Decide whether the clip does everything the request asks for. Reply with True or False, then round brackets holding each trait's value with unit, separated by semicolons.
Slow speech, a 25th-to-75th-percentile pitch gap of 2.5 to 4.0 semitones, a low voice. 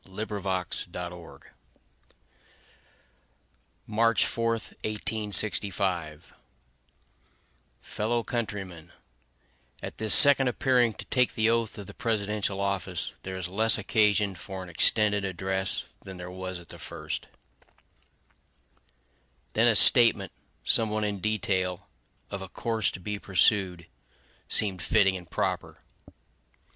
True (115 wpm; 2.9 semitones; 100 Hz)